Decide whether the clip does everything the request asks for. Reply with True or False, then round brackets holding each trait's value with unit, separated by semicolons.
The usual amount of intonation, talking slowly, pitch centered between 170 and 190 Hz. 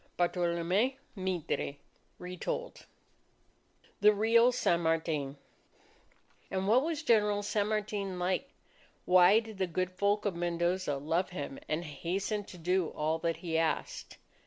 True (3.6 semitones; 130 wpm; 185 Hz)